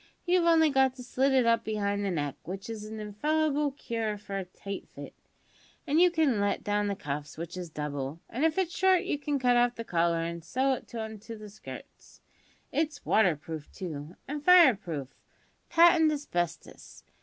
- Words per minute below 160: No, average, 195 wpm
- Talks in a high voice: Yes, high, 220 Hz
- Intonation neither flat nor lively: No, wide, 8.6 semitones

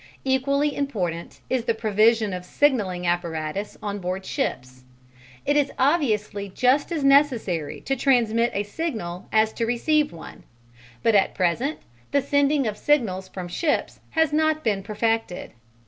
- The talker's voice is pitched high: Yes, high, 225 Hz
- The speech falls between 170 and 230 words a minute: No, average, 145 wpm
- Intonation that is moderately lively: No, wide, 6.8 semitones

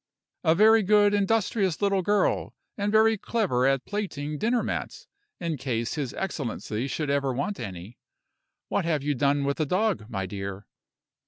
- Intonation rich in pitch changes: Yes, wide, 7.8 semitones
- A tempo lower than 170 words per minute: Yes, average, 160 wpm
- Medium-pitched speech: Yes, medium, 155 Hz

